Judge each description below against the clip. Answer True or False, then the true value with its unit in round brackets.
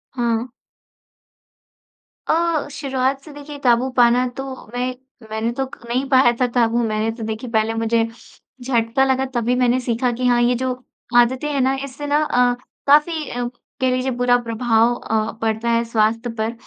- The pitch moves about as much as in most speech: False (2.3 semitones)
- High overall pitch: True (245 Hz)